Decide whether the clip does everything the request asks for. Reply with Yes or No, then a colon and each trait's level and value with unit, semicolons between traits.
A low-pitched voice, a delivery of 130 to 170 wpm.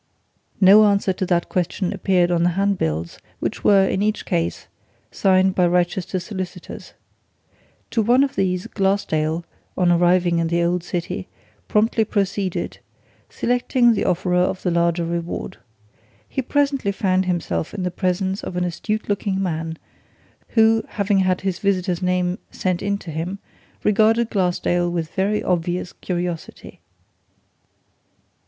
No: medium, 185 Hz; average, 140 wpm